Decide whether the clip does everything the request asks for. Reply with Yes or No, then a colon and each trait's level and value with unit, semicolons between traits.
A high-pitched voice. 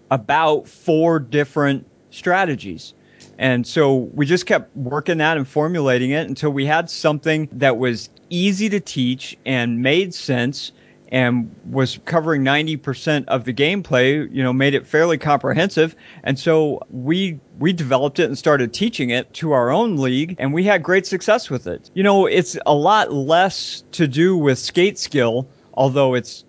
No: medium, 145 Hz